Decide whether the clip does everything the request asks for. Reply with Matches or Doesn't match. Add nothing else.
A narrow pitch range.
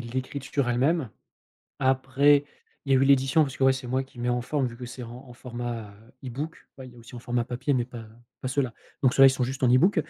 Matches